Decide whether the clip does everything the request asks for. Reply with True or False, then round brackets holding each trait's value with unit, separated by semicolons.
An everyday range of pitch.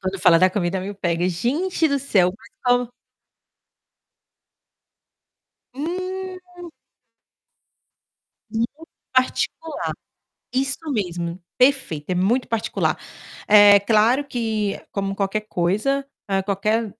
False (6.0 semitones)